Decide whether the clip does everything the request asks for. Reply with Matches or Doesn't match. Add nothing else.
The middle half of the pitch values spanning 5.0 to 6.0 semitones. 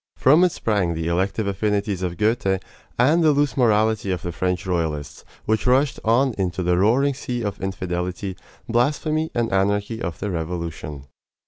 Matches